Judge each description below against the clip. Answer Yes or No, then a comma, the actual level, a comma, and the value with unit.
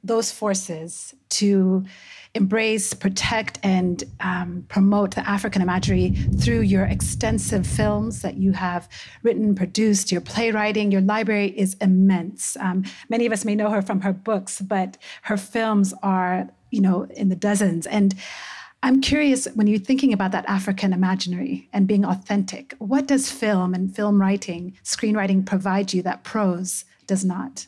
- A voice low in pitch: No, high, 195 Hz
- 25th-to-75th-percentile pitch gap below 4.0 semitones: Yes, narrow, 2.4 semitones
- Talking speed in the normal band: Yes, average, 155 wpm